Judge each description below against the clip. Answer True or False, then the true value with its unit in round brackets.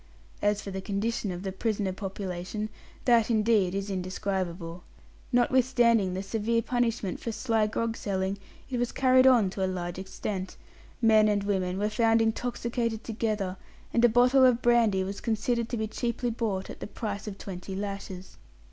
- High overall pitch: True (210 Hz)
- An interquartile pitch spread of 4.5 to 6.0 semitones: False (3.4 semitones)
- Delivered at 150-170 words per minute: True (165 wpm)